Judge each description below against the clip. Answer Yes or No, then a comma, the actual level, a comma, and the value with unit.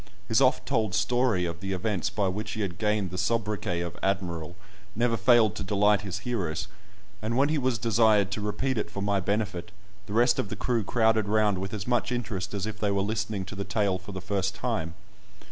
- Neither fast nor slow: No, fast, 215 wpm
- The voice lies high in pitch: No, low, 105 Hz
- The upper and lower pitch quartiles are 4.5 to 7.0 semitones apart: No, average, 2.7 semitones